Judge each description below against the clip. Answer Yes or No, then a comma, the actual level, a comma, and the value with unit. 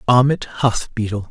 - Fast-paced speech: No, average, 140 wpm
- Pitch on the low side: Yes, low, 115 Hz